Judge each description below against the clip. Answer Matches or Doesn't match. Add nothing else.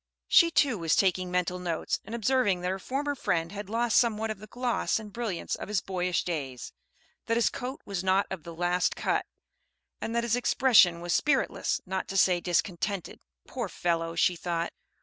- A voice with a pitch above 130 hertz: Matches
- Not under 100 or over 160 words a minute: Doesn't match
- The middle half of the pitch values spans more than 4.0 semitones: Matches